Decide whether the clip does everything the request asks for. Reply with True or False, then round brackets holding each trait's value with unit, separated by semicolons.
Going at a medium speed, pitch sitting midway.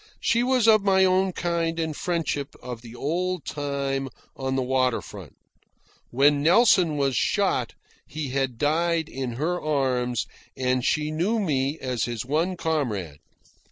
True (150 wpm; 145 Hz)